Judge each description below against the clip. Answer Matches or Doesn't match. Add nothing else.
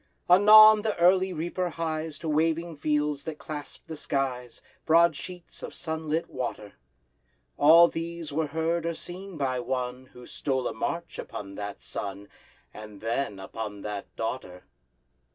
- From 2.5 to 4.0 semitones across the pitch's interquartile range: Doesn't match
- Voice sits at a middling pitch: Matches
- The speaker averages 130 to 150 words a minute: Matches